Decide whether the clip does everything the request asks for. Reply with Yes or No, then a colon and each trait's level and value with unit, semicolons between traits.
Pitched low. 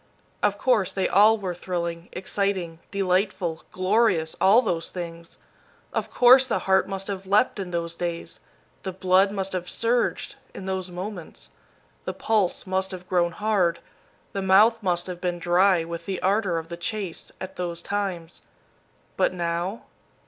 No: medium, 185 Hz